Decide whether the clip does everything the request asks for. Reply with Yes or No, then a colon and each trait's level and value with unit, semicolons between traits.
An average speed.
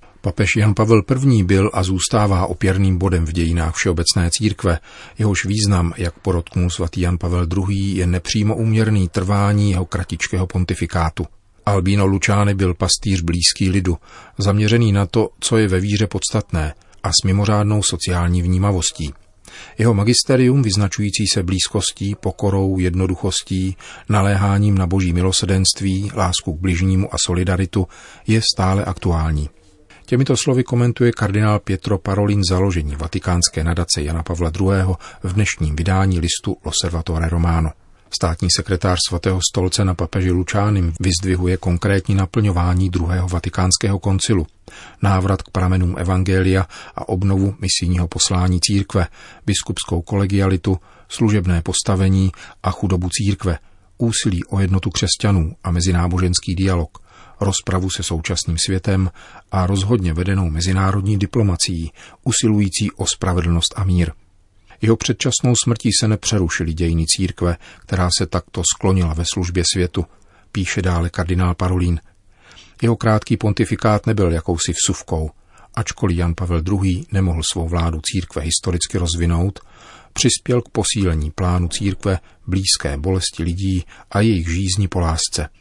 Yes: average, 125 wpm